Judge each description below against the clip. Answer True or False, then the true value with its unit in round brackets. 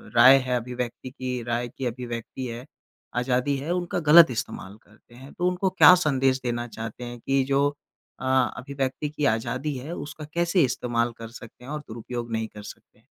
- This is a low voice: True (125 Hz)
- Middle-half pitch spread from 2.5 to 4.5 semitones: True (3.3 semitones)